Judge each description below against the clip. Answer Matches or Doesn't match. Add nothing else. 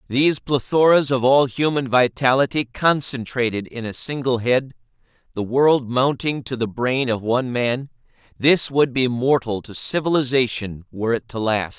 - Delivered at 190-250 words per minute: Doesn't match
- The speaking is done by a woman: Doesn't match